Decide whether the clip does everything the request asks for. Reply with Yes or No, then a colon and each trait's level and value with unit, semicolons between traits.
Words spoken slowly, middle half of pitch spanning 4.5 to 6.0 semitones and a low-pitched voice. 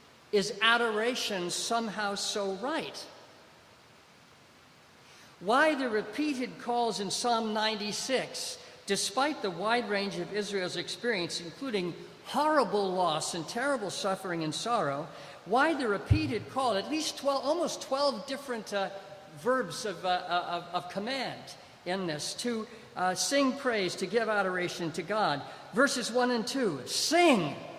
No: slow, 130 wpm; average, 5.1 semitones; high, 210 Hz